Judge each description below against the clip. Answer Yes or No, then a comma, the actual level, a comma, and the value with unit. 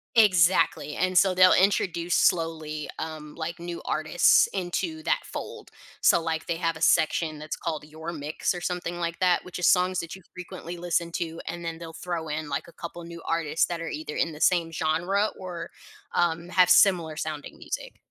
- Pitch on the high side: No, medium, 170 Hz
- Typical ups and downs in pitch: No, narrow, 1.9 semitones